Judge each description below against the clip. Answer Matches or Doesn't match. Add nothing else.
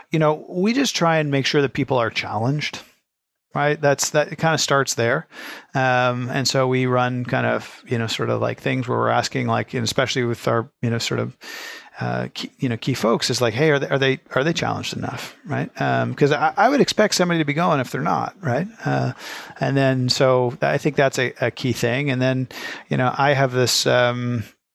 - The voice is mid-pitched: Doesn't match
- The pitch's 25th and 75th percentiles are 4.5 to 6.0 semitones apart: Doesn't match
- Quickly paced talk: Matches